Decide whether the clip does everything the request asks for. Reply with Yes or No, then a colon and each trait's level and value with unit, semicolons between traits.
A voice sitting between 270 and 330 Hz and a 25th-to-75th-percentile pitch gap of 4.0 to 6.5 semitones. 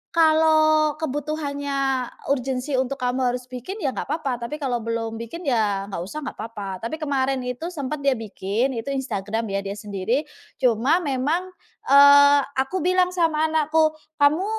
Yes: very high, 275 Hz; average, 4.7 semitones